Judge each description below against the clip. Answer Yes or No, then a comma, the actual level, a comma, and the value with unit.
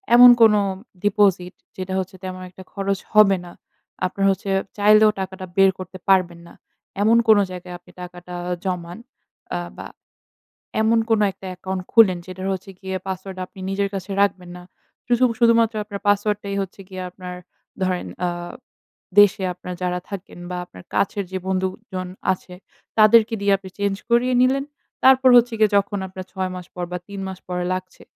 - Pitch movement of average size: No, narrow, 2.0 semitones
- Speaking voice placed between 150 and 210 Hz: Yes, high, 190 Hz